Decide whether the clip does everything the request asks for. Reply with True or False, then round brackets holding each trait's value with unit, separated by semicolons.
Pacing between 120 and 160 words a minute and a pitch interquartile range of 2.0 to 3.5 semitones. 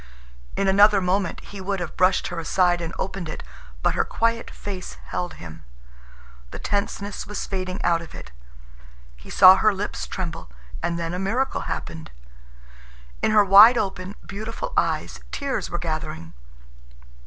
True (155 wpm; 2.8 semitones)